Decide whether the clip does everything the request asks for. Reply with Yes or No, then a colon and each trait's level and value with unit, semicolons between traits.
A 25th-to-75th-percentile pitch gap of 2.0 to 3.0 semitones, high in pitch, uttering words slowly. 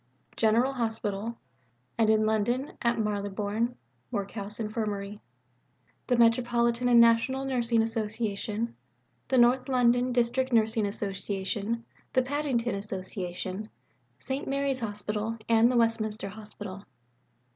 Yes: narrow, 2.5 semitones; high, 225 Hz; slow, 105 wpm